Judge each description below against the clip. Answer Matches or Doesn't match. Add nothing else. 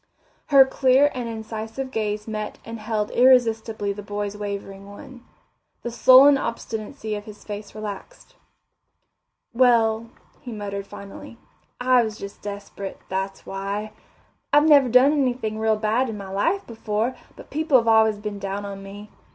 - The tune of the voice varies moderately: Matches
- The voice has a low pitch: Doesn't match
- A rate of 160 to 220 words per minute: Doesn't match